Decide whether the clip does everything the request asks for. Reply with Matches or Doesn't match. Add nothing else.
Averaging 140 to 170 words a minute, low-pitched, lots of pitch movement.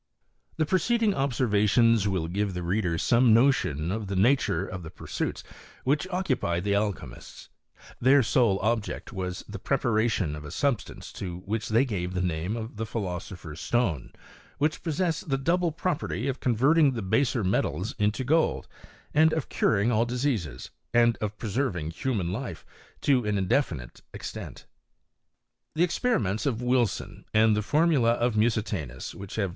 Matches